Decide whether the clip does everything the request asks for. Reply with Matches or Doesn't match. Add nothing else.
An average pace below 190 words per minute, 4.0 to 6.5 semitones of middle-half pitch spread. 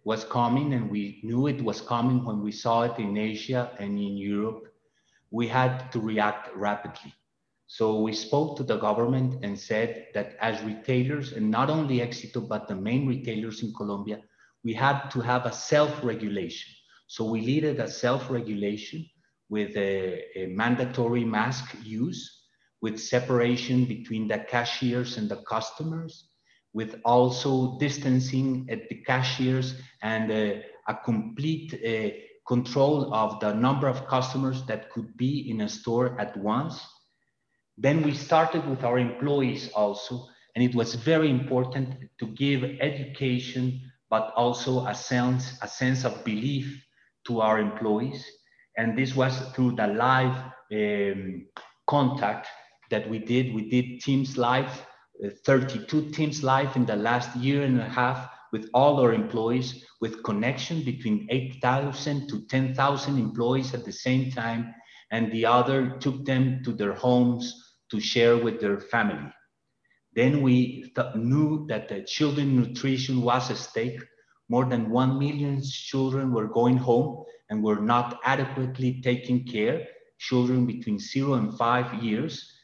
Doesn't match